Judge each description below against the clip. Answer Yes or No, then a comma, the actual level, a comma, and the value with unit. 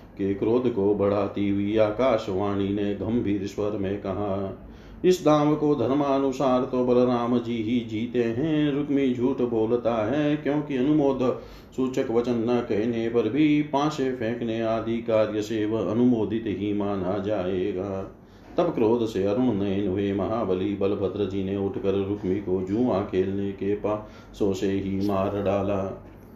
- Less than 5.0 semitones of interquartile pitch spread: Yes, average, 3.8 semitones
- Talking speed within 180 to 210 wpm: No, average, 140 wpm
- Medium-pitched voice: No, low, 110 Hz